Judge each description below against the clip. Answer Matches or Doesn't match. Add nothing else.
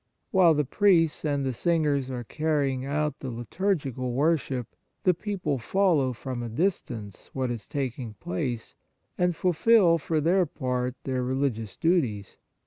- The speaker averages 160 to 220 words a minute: Doesn't match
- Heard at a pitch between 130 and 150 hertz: Matches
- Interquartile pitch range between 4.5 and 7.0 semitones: Matches